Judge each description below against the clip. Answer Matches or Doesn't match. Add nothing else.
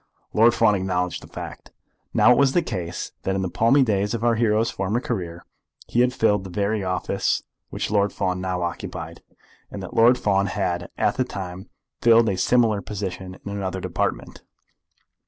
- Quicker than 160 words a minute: Matches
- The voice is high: Doesn't match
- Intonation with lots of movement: Doesn't match